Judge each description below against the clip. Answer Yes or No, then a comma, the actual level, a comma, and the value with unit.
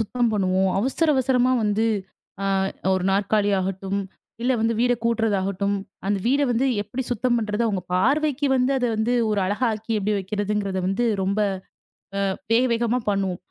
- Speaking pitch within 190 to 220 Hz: Yes, high, 215 Hz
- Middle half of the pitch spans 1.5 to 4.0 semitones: Yes, average, 3.7 semitones